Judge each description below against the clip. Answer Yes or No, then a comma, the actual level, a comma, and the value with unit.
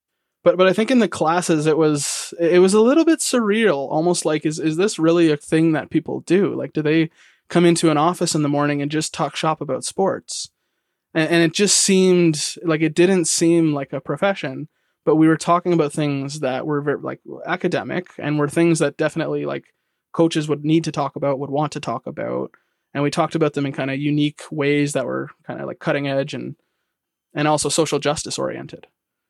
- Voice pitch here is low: No, medium, 155 Hz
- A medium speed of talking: No, fast, 215 wpm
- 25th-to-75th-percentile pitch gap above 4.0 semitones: No, narrow, 2.6 semitones